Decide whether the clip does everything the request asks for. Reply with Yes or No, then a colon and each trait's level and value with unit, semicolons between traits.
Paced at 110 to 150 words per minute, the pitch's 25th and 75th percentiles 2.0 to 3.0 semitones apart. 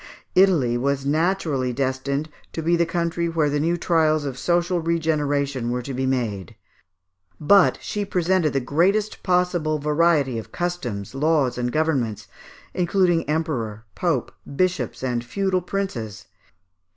No: slow, 135 wpm; average, 4.9 semitones